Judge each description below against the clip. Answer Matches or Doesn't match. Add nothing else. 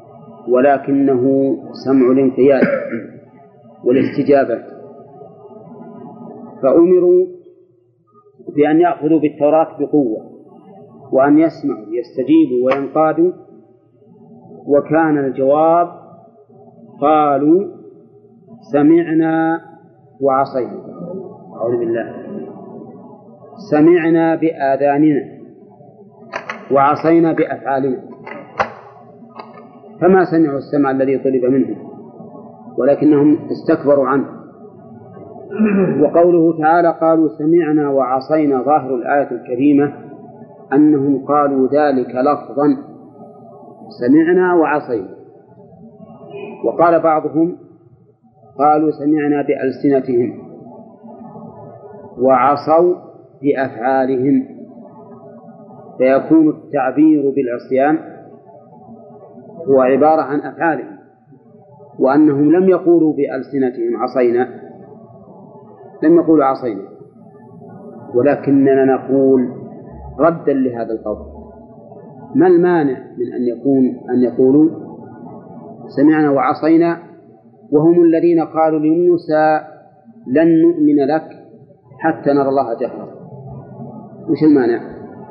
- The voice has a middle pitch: Matches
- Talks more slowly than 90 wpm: Matches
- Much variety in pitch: Doesn't match